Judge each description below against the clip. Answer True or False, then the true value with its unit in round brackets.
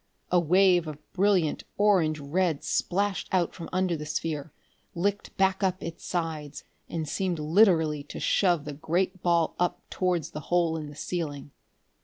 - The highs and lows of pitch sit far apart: False (3.3 semitones)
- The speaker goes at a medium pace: True (160 wpm)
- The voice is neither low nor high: True (170 Hz)